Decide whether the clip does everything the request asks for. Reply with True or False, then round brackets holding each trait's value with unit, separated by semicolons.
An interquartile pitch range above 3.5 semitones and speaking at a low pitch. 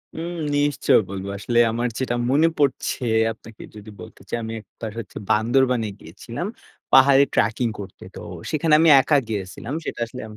True (4.3 semitones; 120 Hz)